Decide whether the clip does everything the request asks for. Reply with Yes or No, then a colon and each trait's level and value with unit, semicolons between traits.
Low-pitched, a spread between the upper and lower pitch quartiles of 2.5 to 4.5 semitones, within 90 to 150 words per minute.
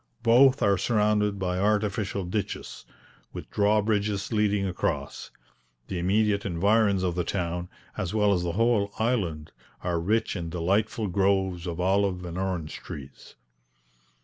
Yes: low, 100 Hz; average, 2.9 semitones; average, 140 wpm